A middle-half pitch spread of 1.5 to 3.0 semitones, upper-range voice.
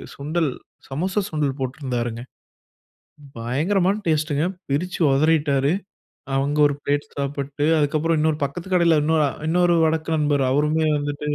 No: narrow, 2.4 semitones; medium, 150 Hz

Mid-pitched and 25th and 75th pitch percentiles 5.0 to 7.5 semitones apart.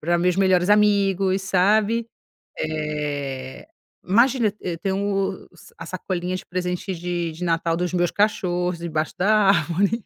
No: medium, 180 Hz; average, 2.7 semitones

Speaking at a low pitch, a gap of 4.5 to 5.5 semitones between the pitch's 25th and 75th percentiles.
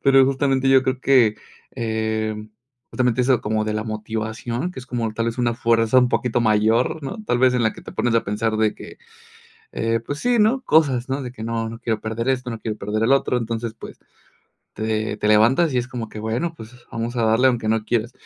No: low, 115 Hz; average, 2.8 semitones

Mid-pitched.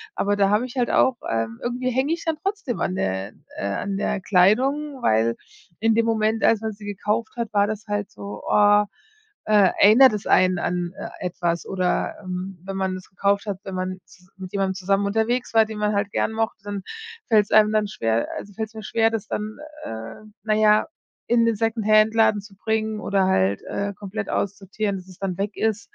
No: high, 205 Hz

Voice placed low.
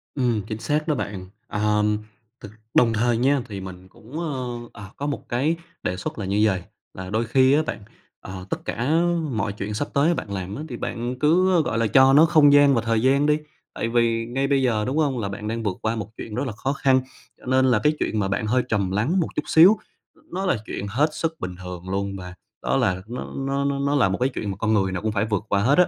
Yes: low, 115 Hz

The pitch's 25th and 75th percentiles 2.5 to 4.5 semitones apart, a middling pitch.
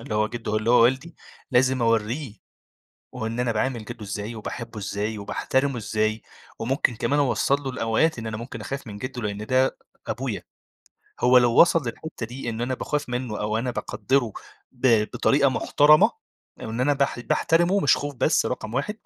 No: average, 3.4 semitones; low, 120 Hz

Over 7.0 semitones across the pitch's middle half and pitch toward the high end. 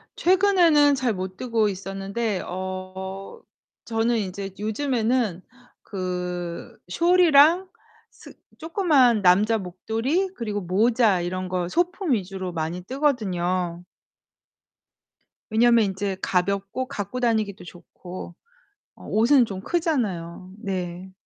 No: wide, 5.4 semitones; high, 205 Hz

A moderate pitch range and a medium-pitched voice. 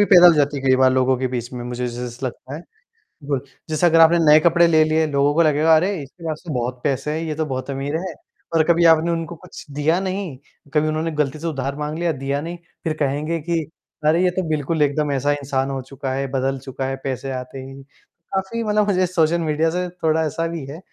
Yes: average, 3.5 semitones; medium, 150 Hz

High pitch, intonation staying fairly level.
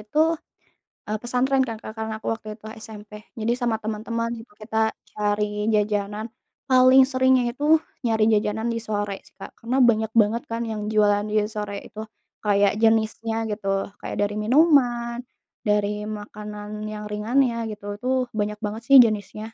Yes: high, 220 Hz; narrow, 2.1 semitones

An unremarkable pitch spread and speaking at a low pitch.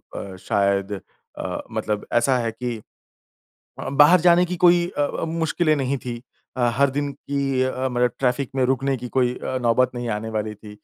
Yes: average, 3.1 semitones; low, 130 Hz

